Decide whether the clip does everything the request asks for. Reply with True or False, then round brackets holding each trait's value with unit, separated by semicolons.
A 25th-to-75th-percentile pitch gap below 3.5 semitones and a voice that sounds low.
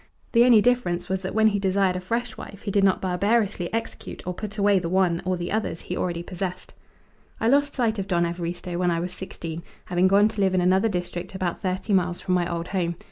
False (2.7 semitones; 185 Hz)